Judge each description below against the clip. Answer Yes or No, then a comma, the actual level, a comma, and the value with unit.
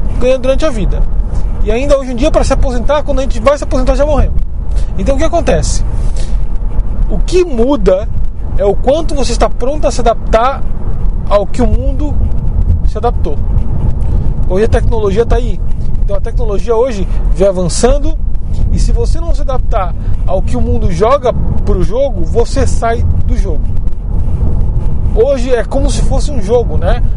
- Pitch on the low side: Yes, low, 115 Hz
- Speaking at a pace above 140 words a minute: Yes, average, 170 wpm